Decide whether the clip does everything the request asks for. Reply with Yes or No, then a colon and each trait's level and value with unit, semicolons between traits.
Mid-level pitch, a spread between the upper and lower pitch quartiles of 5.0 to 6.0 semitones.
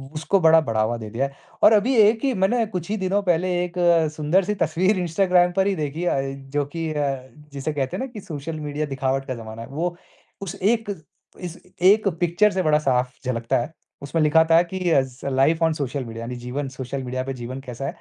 Yes: medium, 150 Hz; average, 5.3 semitones